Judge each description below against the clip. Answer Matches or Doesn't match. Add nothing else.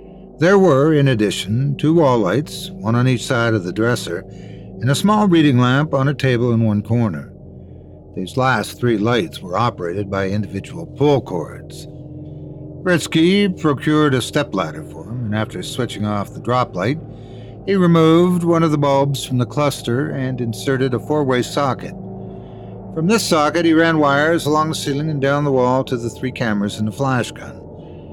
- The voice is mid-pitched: Doesn't match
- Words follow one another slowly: Doesn't match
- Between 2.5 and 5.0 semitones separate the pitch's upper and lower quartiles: Doesn't match